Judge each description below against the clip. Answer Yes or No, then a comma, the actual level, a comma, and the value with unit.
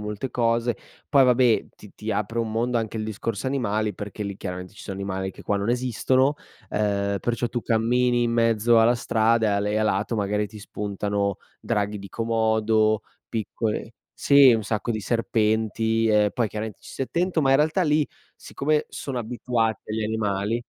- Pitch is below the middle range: Yes, low, 110 Hz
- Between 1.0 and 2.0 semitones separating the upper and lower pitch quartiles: No, narrow, 2.4 semitones